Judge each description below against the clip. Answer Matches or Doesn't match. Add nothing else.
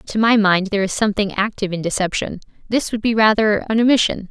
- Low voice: Doesn't match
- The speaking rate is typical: Doesn't match